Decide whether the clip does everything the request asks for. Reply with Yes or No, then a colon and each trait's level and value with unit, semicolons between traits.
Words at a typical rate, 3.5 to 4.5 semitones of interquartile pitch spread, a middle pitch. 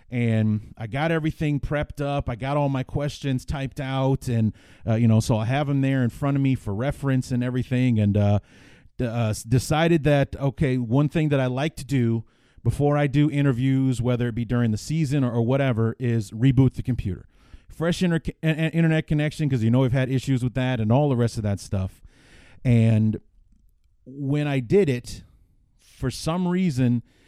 No: average, 195 wpm; average, 4.0 semitones; low, 130 Hz